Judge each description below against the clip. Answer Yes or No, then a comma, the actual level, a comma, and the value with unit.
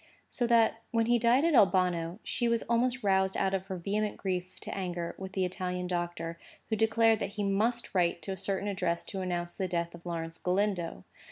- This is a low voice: No, high, 190 Hz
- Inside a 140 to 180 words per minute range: No, fast, 205 wpm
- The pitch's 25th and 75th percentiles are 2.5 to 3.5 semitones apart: No, average, 3.9 semitones